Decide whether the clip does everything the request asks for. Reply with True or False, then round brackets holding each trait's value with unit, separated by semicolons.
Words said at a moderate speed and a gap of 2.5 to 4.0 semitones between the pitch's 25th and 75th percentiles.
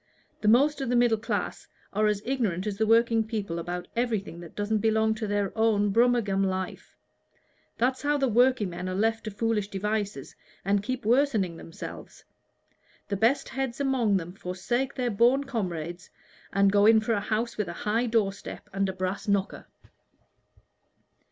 True (170 wpm; 3.3 semitones)